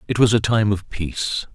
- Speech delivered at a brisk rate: Yes, fast, 235 wpm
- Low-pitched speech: Yes, low, 105 Hz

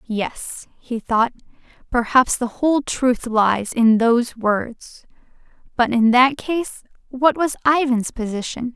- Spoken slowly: Yes, slow, 130 wpm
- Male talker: No, female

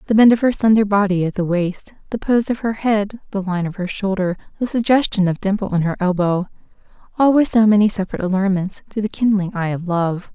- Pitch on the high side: Yes, high, 200 Hz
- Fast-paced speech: Yes, fast, 215 wpm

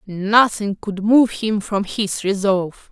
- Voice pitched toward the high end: Yes, high, 205 Hz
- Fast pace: No, average, 145 wpm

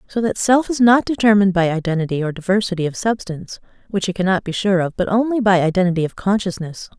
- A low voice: No, high, 195 Hz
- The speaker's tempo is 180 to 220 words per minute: Yes, fast, 205 wpm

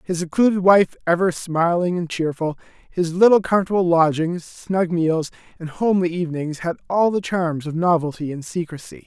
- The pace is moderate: Yes, average, 160 wpm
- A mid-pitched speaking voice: Yes, medium, 170 Hz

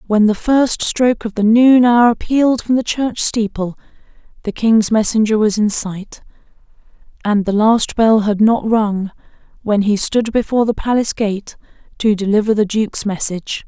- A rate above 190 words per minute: No, average, 165 wpm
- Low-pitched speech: No, high, 220 Hz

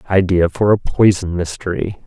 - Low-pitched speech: Yes, very low, 95 Hz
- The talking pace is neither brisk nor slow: Yes, average, 145 wpm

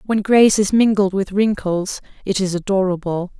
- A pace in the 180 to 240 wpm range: No, average, 160 wpm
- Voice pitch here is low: No, high, 195 Hz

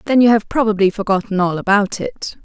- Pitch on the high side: Yes, high, 205 Hz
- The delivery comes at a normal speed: Yes, average, 195 wpm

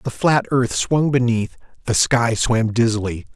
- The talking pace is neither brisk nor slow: Yes, average, 160 wpm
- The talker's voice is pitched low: Yes, low, 120 Hz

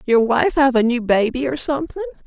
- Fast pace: Yes, fast, 210 wpm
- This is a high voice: Yes, very high, 255 Hz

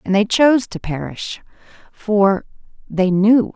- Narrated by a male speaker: No, female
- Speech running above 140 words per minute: No, slow, 135 wpm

